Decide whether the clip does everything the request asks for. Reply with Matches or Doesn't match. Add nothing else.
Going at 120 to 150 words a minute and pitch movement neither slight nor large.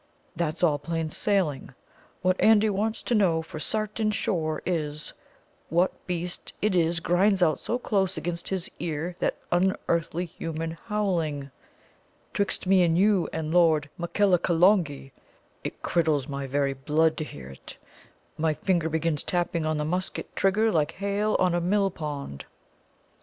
Matches